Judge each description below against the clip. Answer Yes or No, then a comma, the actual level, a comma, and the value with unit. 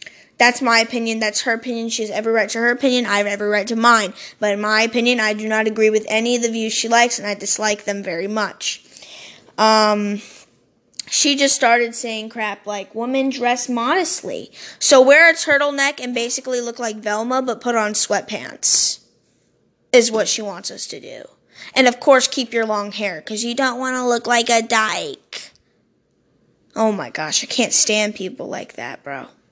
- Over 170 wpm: Yes, average, 190 wpm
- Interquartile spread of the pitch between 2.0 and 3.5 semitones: Yes, narrow, 2.6 semitones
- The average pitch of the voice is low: No, high, 230 Hz